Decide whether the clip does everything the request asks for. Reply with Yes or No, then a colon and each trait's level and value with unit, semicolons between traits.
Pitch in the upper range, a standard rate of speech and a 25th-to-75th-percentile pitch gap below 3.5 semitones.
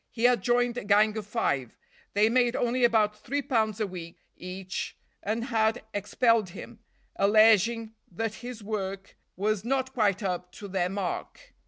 Yes: high, 215 Hz; average, 160 wpm; average, 3.1 semitones